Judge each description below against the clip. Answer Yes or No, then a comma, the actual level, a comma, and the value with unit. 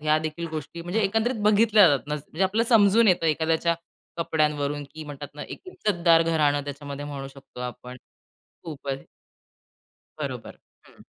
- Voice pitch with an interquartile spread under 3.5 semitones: No, average, 4.6 semitones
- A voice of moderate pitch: Yes, medium, 155 Hz